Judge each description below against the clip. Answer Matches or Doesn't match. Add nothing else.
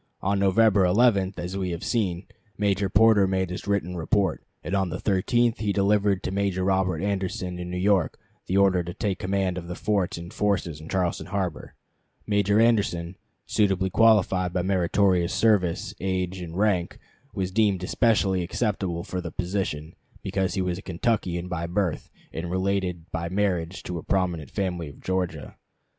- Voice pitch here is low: Matches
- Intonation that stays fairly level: Matches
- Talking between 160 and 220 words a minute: Matches